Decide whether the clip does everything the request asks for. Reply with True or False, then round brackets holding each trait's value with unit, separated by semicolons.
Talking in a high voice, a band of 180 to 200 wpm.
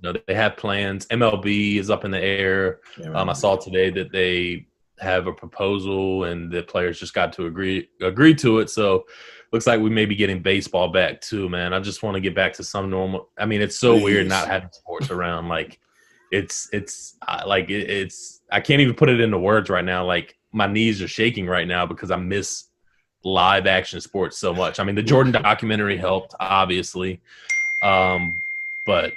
False (100 Hz; 195 wpm)